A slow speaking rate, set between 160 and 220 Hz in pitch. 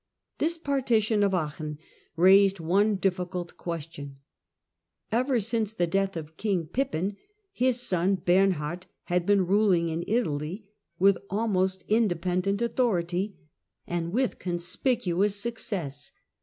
Yes: slow, 115 wpm; high, 190 Hz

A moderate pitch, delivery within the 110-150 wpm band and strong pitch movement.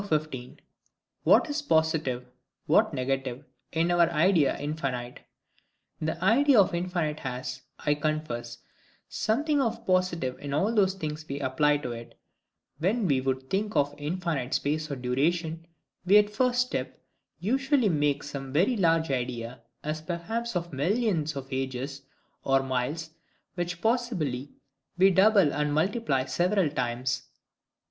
Yes: medium, 155 Hz; average, 140 wpm; wide, 5.9 semitones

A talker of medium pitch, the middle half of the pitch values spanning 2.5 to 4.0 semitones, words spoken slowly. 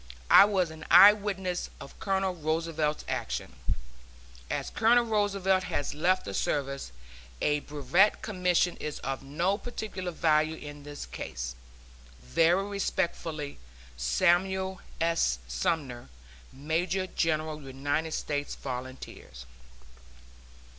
No: medium, 160 Hz; average, 4.7 semitones; slow, 105 wpm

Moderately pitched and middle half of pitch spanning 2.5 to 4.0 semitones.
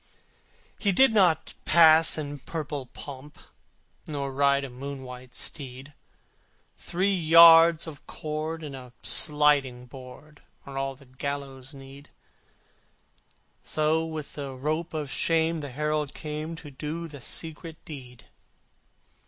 Yes: medium, 150 Hz; average, 2.9 semitones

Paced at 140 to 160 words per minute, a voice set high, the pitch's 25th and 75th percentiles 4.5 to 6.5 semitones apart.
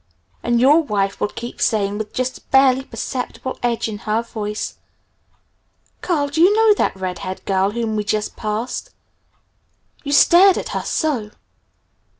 Yes: average, 155 wpm; high, 235 Hz; average, 5.1 semitones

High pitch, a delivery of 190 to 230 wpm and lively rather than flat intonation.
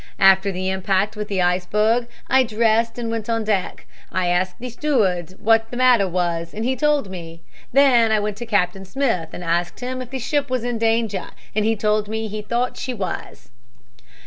No: high, 215 Hz; average, 200 wpm; average, 4.2 semitones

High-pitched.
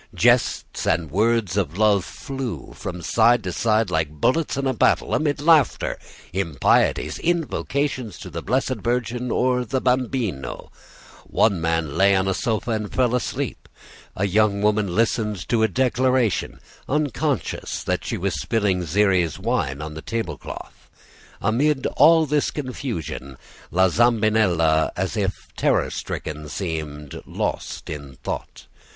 No: low, 110 Hz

